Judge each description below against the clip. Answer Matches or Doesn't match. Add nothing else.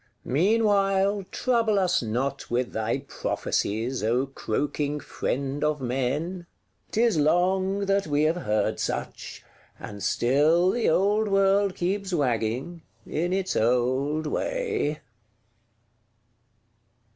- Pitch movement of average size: Doesn't match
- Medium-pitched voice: Matches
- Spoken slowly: Matches